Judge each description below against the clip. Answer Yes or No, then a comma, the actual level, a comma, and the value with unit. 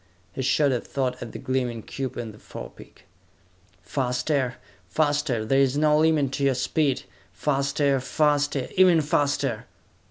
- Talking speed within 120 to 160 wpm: Yes, average, 140 wpm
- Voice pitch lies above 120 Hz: Yes, low, 135 Hz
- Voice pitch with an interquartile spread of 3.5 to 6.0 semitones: No, average, 2.7 semitones